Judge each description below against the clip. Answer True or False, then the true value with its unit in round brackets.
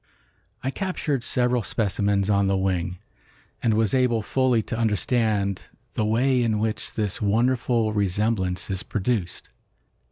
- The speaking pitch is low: True (110 Hz)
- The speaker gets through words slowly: True (130 wpm)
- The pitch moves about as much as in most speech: True (3.6 semitones)